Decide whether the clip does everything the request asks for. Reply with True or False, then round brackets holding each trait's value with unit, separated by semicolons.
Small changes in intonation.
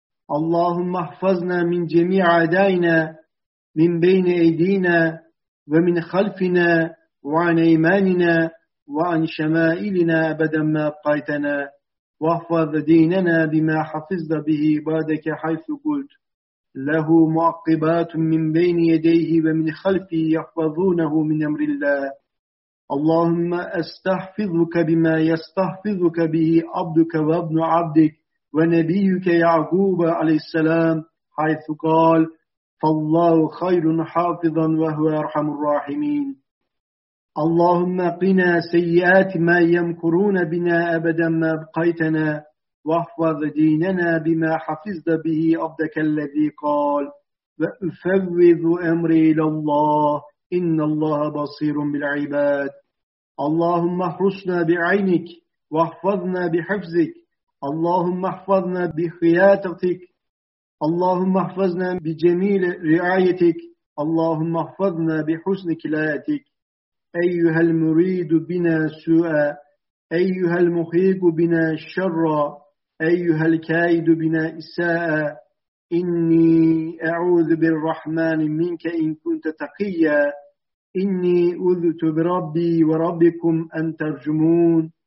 True (1.7 semitones)